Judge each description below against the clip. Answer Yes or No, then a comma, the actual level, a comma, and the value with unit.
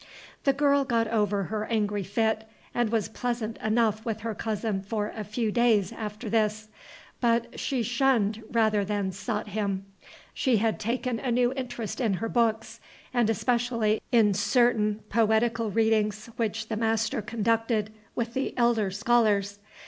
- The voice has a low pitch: No, high, 220 Hz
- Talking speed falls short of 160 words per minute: Yes, average, 150 wpm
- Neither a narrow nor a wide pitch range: No, narrow, 2.0 semitones